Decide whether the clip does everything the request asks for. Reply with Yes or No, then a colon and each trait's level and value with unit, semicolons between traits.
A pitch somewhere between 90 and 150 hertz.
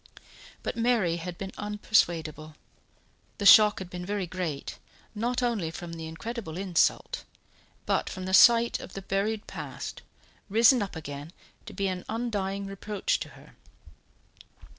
No: high, 195 Hz